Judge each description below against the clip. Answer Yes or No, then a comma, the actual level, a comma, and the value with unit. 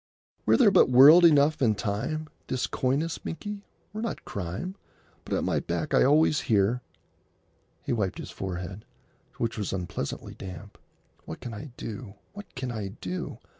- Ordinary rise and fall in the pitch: No, wide, 7.6 semitones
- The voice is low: Yes, low, 120 Hz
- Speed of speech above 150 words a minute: Yes, average, 160 wpm